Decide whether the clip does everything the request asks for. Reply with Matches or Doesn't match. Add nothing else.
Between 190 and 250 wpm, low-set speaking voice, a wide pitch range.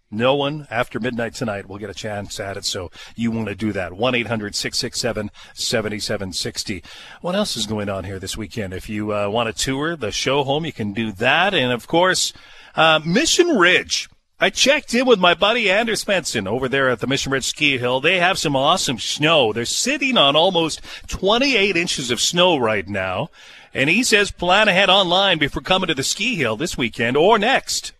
Matches